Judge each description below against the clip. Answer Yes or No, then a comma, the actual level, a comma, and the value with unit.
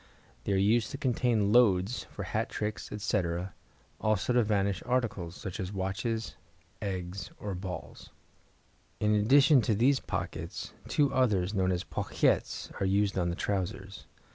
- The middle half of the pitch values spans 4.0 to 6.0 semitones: No, average, 3.3 semitones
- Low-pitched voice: Yes, low, 100 Hz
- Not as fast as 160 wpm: Yes, average, 145 wpm